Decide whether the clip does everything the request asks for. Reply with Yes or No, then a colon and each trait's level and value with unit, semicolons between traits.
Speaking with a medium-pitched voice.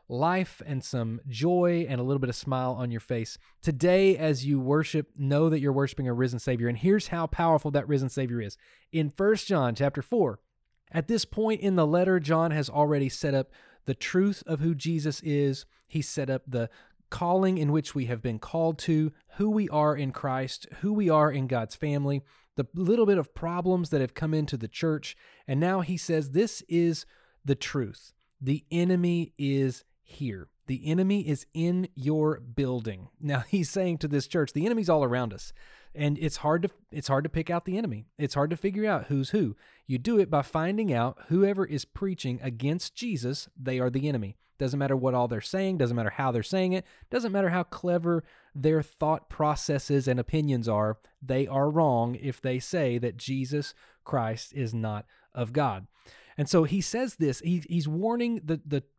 Yes: medium, 150 Hz